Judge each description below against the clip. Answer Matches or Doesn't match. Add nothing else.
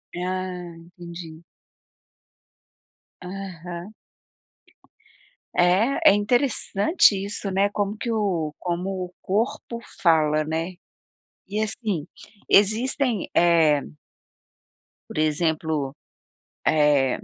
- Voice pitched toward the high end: Doesn't match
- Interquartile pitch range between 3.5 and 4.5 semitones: Matches